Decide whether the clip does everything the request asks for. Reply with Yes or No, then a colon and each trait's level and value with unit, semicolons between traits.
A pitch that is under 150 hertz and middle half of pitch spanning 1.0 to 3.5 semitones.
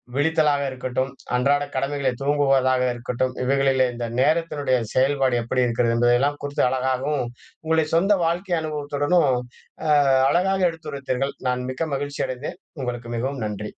Yes: low, 135 Hz; narrow, 2.5 semitones